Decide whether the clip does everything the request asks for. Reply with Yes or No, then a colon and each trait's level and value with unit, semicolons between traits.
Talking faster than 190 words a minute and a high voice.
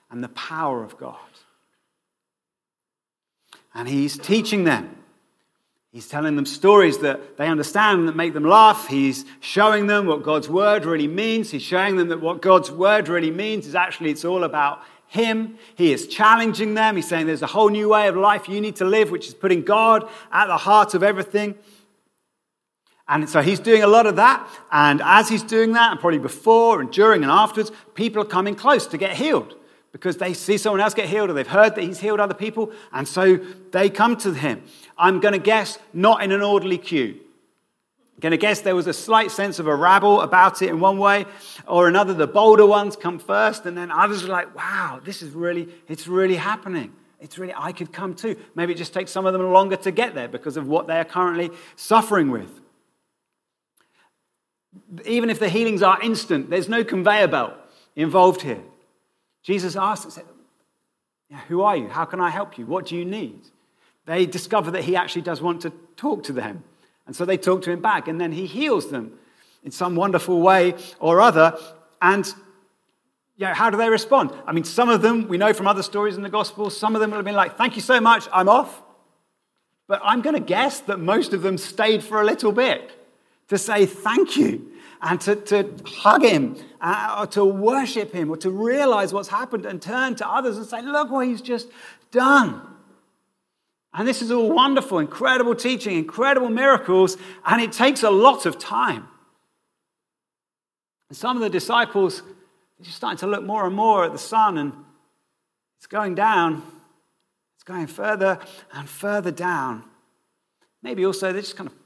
Yes: average, 200 wpm; high, 195 Hz